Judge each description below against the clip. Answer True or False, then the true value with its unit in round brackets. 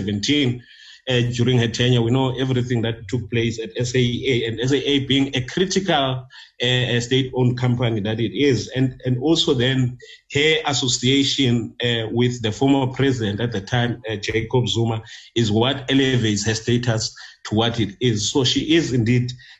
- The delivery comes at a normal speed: True (160 wpm)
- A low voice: True (125 Hz)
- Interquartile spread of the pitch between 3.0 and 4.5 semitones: False (2.4 semitones)